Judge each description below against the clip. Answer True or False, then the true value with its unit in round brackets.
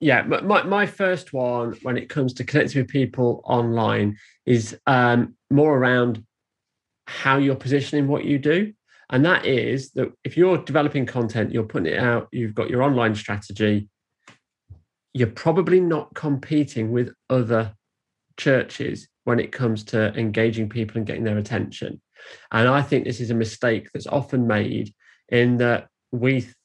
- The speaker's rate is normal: True (160 wpm)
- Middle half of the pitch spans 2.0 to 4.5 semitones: True (3.8 semitones)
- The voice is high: False (125 Hz)